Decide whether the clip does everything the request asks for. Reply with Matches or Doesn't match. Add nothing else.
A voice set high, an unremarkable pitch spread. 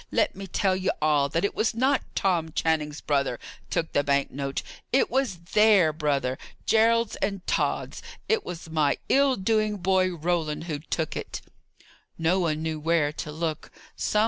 Doesn't match